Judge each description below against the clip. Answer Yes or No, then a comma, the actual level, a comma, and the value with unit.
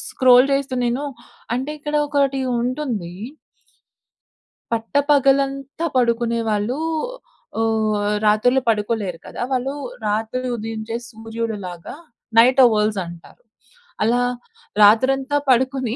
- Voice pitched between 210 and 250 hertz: Yes, high, 235 Hz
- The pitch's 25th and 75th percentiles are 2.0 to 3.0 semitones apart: No, average, 3.5 semitones